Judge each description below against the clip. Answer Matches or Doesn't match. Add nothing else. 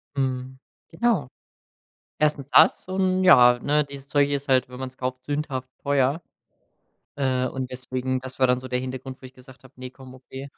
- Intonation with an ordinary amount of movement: Doesn't match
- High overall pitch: Doesn't match